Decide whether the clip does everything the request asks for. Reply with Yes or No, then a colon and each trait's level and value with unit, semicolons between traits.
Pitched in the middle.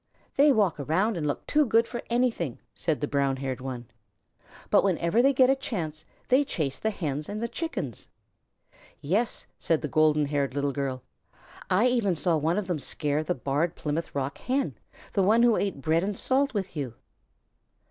Yes: medium, 170 Hz